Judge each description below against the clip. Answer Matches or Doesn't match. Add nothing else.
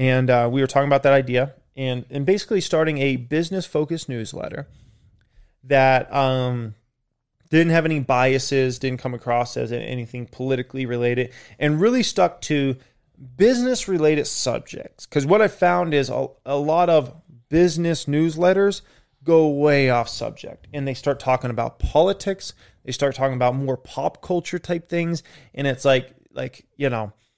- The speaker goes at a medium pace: Matches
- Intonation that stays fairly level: Doesn't match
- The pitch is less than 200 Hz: Matches